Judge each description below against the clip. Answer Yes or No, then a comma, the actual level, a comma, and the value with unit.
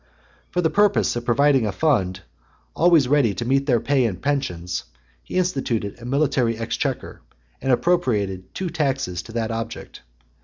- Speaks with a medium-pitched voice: No, low, 125 Hz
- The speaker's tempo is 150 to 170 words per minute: Yes, average, 155 wpm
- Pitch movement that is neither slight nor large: Yes, average, 4.6 semitones